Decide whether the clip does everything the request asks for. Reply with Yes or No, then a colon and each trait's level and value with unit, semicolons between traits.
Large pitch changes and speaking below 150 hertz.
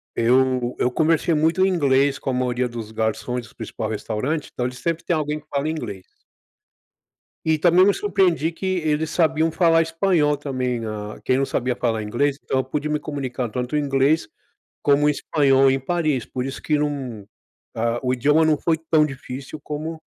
No: average, 4.0 semitones; medium, 140 Hz